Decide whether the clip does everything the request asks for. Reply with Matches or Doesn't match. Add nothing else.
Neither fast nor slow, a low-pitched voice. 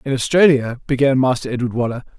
Matches